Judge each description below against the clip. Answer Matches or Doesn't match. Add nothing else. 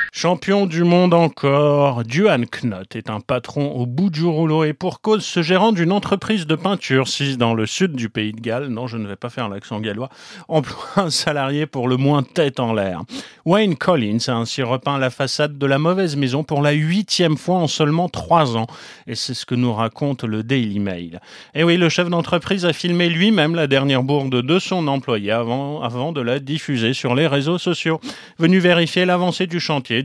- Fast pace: Doesn't match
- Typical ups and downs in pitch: Doesn't match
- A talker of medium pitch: Matches